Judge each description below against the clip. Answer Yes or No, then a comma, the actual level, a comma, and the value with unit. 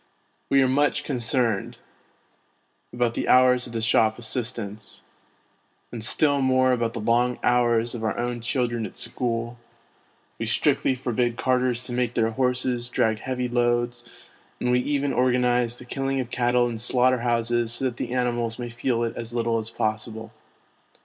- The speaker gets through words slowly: No, average, 165 wpm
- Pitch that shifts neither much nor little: No, narrow, 1.5 semitones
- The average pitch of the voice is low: Yes, low, 120 Hz